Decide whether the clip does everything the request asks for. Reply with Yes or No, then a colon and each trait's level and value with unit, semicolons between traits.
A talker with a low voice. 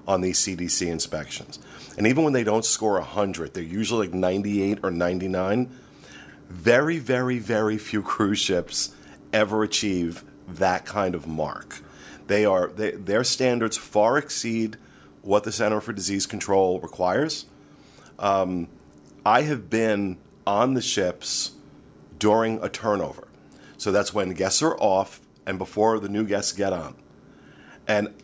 Yes: low, 100 Hz